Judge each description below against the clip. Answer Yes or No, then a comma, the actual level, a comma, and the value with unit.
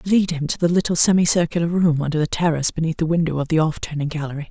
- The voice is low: No, medium, 160 Hz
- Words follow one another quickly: Yes, fast, 255 wpm